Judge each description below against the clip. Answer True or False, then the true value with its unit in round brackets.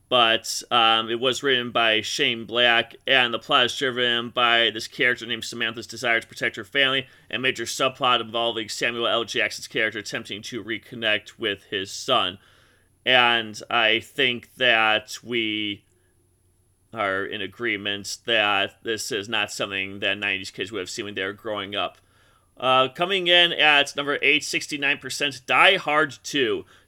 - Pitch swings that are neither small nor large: True (3.6 semitones)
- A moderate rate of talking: True (160 wpm)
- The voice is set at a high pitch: False (115 Hz)